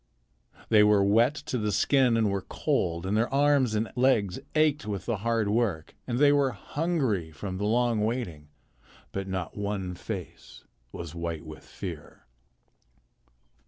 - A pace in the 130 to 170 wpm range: Yes, average, 155 wpm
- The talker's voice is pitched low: Yes, low, 105 Hz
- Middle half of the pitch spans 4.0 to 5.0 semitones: Yes, average, 4.6 semitones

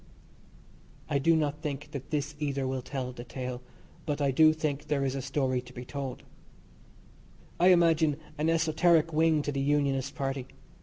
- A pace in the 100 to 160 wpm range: No, average, 170 wpm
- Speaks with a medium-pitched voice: Yes, medium, 145 Hz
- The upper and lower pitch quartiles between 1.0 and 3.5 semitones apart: Yes, narrow, 2.5 semitones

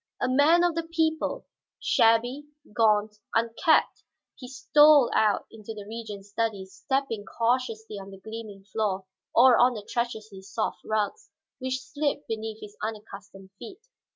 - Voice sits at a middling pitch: No, high, 225 Hz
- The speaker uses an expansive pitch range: No, average, 3.9 semitones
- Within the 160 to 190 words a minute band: No, average, 140 wpm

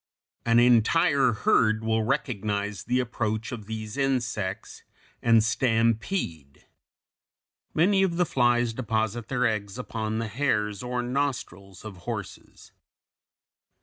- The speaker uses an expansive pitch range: No, average, 2.7 semitones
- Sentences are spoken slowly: Yes, slow, 115 wpm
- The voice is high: No, low, 115 Hz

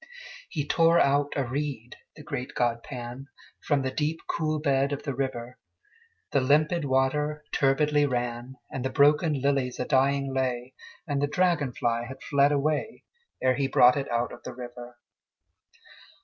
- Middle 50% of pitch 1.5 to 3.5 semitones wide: Yes, average, 2.7 semitones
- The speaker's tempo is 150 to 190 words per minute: Yes, average, 165 wpm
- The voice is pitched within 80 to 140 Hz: Yes, low, 135 Hz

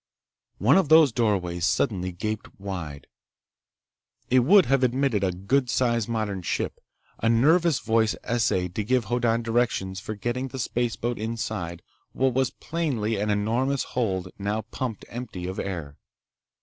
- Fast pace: No, average, 145 wpm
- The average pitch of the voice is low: Yes, low, 115 Hz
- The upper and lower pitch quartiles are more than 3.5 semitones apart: Yes, average, 4.4 semitones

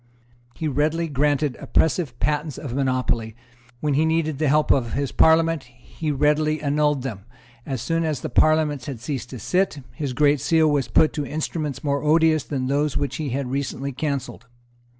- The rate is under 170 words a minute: No, average, 180 wpm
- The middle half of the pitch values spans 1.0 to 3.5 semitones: Yes, narrow, 2.6 semitones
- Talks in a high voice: No, medium, 145 Hz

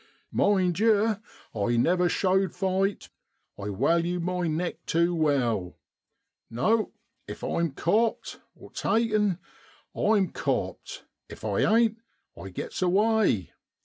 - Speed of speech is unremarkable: No, slow, 110 wpm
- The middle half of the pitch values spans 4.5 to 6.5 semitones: Yes, average, 5.3 semitones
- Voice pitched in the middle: Yes, medium, 180 Hz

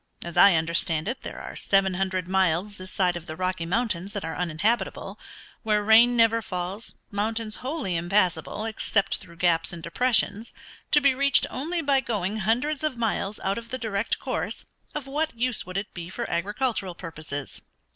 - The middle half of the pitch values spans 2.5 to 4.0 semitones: No, average, 4.6 semitones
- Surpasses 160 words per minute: Yes, average, 175 wpm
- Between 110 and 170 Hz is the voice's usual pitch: No, high, 200 Hz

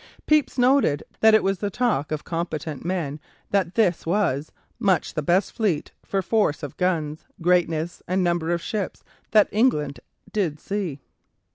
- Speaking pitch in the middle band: Yes, medium, 180 Hz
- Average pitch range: Yes, average, 4.8 semitones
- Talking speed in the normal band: Yes, average, 160 wpm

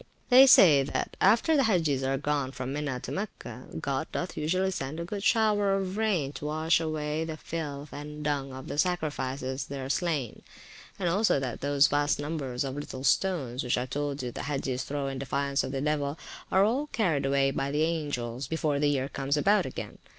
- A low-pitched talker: No, medium, 145 Hz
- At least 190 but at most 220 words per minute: Yes, average, 200 wpm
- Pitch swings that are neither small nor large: Yes, average, 3.7 semitones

